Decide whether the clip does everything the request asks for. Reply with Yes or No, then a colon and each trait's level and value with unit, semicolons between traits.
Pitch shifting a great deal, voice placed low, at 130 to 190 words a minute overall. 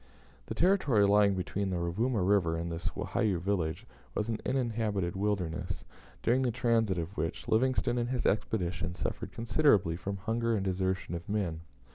No: average, 4.6 semitones; low, 100 Hz; average, 160 wpm